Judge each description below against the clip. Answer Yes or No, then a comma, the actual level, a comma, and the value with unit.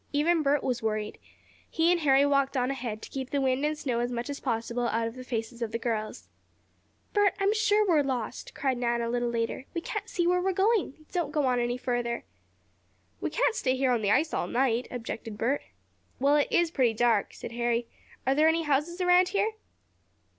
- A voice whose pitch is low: No, very high, 265 Hz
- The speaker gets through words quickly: Yes, fast, 210 wpm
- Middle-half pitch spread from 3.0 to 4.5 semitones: No, average, 5.2 semitones